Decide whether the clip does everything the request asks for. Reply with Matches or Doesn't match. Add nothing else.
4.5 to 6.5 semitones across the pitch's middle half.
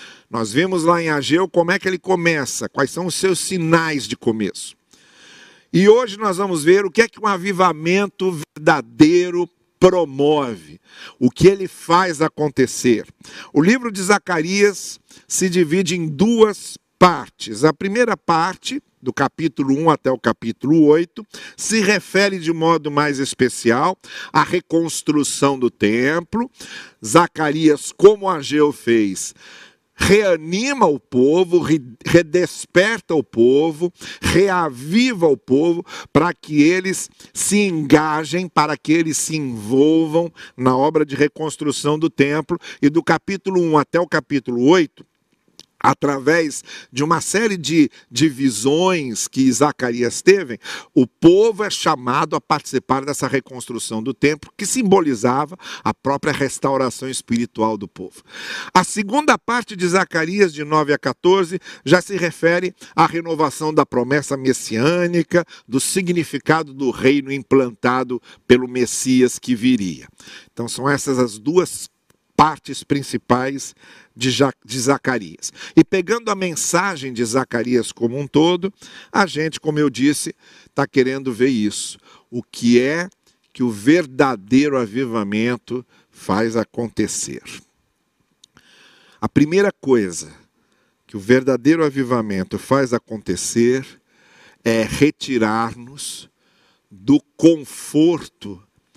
Matches